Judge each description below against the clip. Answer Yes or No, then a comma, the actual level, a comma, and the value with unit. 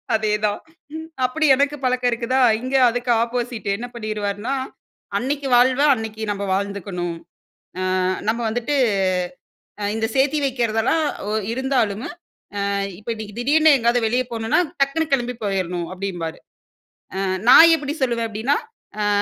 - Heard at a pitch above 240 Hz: No, high, 235 Hz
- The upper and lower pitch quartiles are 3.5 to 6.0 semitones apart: Yes, average, 3.8 semitones